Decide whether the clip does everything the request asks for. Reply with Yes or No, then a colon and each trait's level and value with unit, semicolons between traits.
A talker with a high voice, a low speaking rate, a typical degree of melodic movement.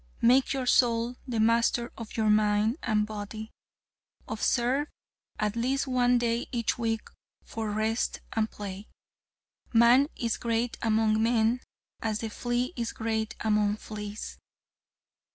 No: high, 225 Hz; slow, 130 wpm; narrow, 1.9 semitones